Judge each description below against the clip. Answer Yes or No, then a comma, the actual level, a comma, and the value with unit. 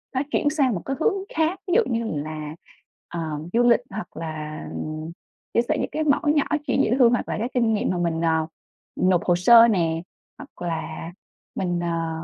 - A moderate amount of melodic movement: No, wide, 7.0 semitones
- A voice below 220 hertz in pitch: Yes, high, 190 Hz